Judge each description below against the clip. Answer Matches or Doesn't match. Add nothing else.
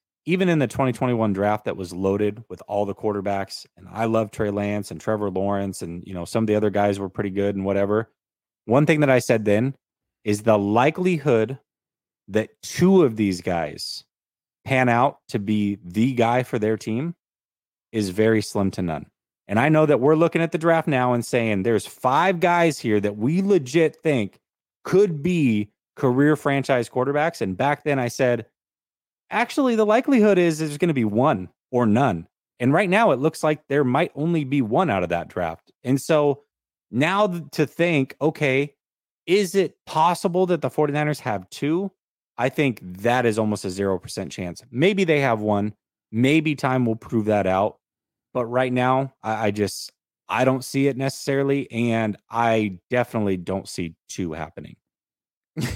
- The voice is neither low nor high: Doesn't match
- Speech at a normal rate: Matches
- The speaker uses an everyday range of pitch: Doesn't match